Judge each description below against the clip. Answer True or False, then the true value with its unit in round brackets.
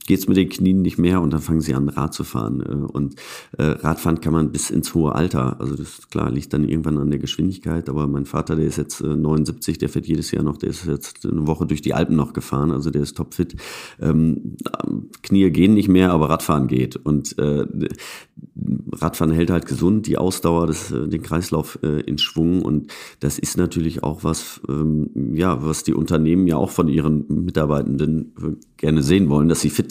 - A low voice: True (80 Hz)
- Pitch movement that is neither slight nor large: False (2.1 semitones)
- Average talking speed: False (195 wpm)